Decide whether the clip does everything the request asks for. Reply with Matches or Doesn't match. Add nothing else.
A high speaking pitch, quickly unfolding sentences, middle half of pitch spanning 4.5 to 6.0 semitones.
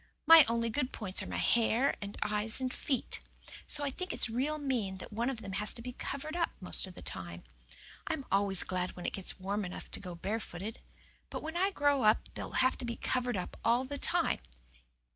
Matches